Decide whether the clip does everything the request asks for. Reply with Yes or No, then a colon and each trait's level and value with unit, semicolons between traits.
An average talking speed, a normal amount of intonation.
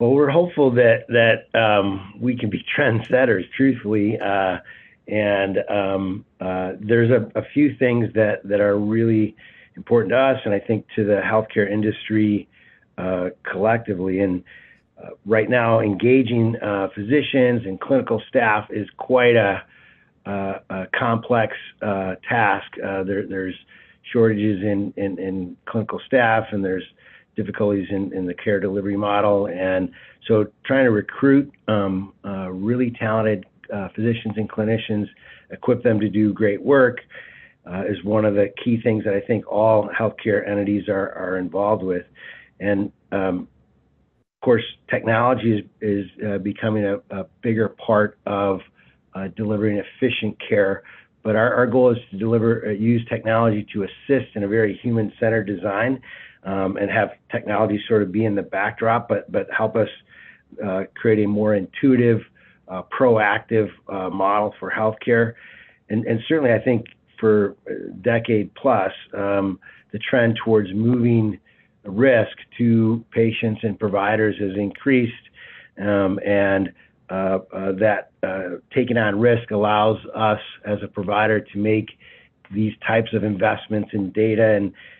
No: average, 150 wpm; narrow, 2.3 semitones